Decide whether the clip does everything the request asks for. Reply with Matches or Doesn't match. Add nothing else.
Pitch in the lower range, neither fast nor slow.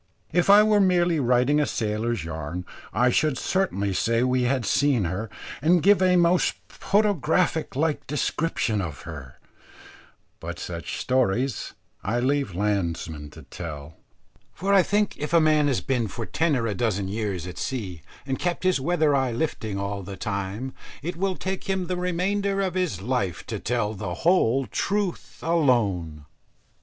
Matches